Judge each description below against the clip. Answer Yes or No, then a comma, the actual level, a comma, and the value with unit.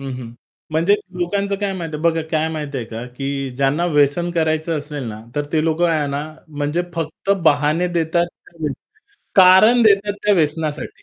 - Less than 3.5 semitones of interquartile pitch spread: Yes, average, 3.1 semitones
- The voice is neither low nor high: Yes, medium, 160 Hz